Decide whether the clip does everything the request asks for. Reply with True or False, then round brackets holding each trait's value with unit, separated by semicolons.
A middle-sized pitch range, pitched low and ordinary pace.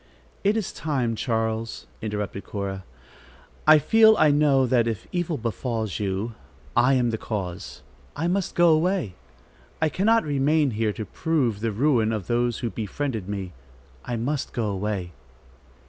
False (6.0 semitones; 120 Hz; 150 wpm)